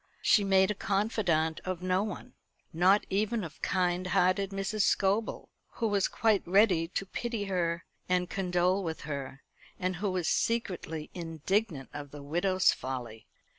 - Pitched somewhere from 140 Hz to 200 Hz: Yes, medium, 185 Hz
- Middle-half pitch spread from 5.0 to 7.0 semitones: No, average, 3.2 semitones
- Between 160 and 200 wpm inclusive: No, average, 150 wpm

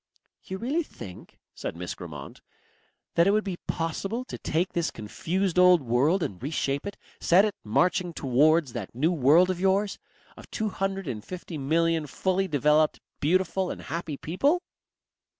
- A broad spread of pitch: No, average, 5.0 semitones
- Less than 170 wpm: Yes, average, 160 wpm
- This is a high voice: No, medium, 170 Hz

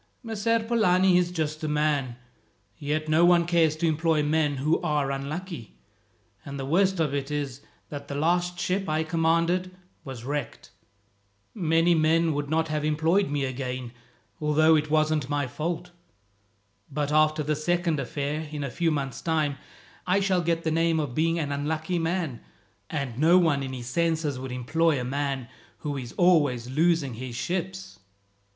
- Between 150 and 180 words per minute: Yes, average, 165 wpm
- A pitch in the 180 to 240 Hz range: No, medium, 155 Hz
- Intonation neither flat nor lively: Yes, average, 3.0 semitones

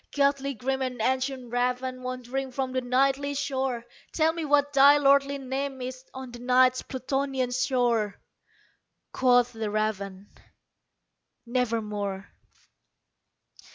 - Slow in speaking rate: Yes, slow, 115 wpm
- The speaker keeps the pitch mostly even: Yes, narrow, 1.9 semitones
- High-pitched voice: Yes, very high, 255 Hz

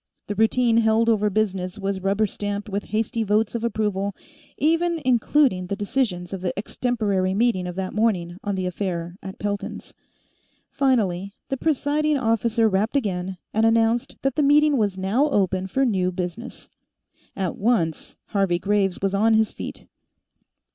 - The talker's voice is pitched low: No, high, 210 Hz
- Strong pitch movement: No, average, 3.6 semitones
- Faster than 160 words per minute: No, average, 155 wpm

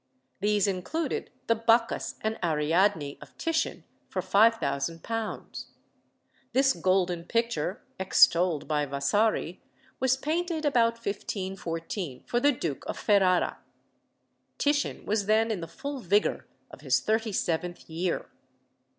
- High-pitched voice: Yes, high, 200 Hz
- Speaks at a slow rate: Yes, slow, 115 wpm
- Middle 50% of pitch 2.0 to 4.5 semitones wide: No, wide, 5.5 semitones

